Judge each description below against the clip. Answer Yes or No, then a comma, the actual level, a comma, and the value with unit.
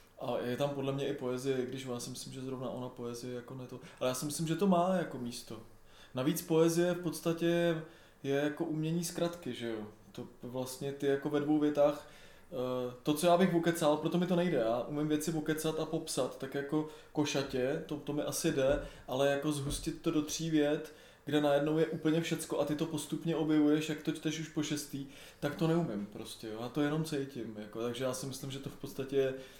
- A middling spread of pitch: Yes, average, 3.6 semitones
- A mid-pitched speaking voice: Yes, medium, 145 Hz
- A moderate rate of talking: No, fast, 220 wpm